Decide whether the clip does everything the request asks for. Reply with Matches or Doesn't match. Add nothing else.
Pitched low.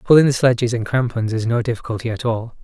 Matches